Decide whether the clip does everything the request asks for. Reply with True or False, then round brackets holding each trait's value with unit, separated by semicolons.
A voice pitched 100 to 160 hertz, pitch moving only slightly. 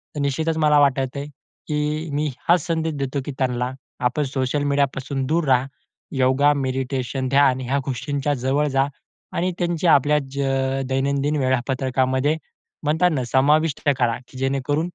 True (140 Hz; 2.2 semitones)